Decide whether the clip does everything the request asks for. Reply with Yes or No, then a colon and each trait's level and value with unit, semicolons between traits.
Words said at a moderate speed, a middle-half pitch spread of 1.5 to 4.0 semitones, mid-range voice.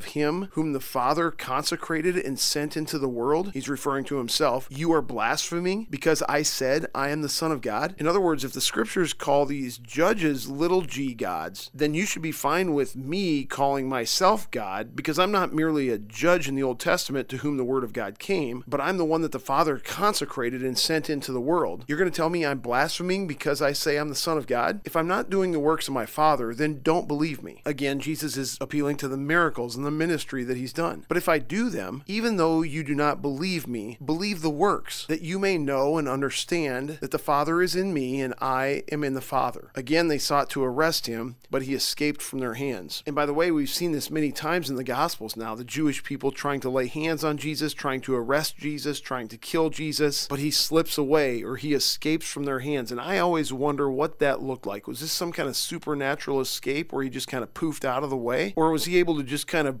No: fast, 240 wpm; average, 3.1 semitones; medium, 145 Hz